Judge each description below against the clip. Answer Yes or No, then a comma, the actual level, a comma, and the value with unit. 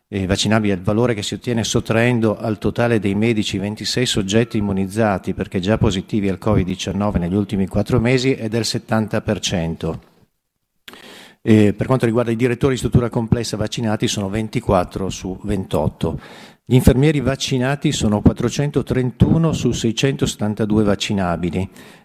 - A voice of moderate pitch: No, low, 110 Hz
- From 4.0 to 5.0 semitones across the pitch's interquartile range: No, average, 3.2 semitones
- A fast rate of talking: No, average, 135 wpm